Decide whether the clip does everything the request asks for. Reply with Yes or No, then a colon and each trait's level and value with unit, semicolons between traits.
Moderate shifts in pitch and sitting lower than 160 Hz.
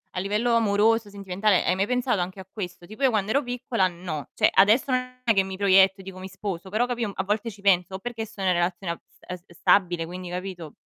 No: average, 3.6 semitones; high, 195 Hz